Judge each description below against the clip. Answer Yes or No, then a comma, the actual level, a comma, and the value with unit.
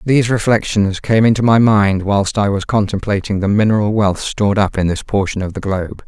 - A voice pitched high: No, low, 105 Hz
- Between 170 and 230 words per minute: Yes, fast, 205 wpm